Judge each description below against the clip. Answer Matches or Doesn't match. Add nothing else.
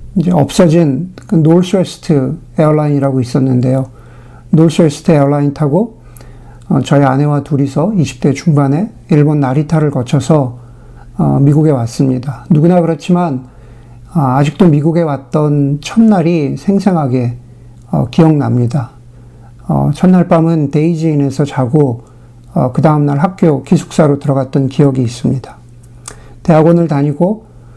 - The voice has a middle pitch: Matches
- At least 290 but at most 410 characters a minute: Doesn't match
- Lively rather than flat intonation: Doesn't match